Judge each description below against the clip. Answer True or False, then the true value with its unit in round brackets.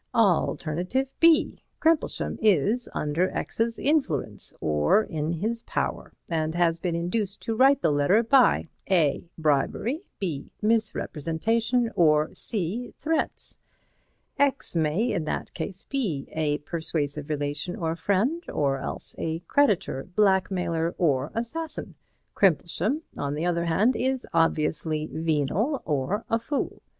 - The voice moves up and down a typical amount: False (6.8 semitones)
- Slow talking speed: True (125 wpm)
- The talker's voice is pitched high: False (175 Hz)